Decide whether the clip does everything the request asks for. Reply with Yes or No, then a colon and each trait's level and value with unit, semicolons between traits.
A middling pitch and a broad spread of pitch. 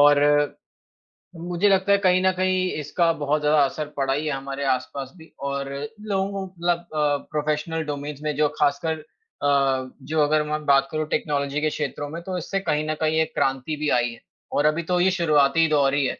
No: medium, 150 Hz; average, 2.8 semitones